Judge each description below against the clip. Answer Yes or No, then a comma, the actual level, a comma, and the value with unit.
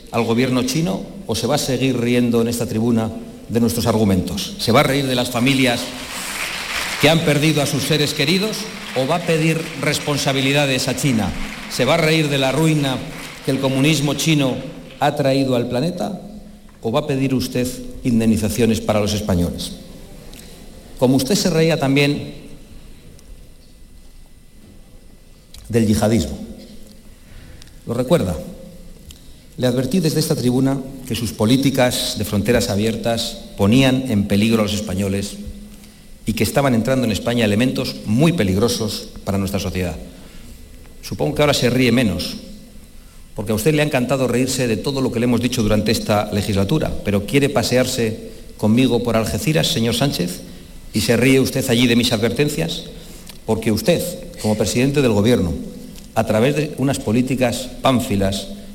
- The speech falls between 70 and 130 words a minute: No, average, 150 wpm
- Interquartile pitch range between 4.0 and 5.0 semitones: Yes, average, 4.4 semitones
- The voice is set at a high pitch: No, low, 125 Hz